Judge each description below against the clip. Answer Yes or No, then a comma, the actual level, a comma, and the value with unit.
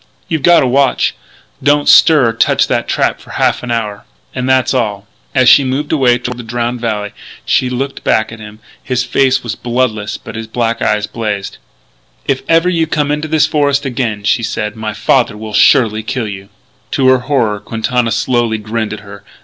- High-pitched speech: No, low, 120 Hz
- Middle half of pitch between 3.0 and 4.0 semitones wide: Yes, average, 3.5 semitones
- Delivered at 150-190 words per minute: No, average, 200 wpm